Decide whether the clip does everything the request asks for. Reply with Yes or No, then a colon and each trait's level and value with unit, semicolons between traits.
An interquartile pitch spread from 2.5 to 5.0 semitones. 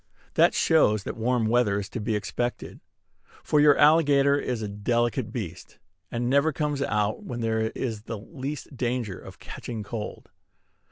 Yes: average, 4.3 semitones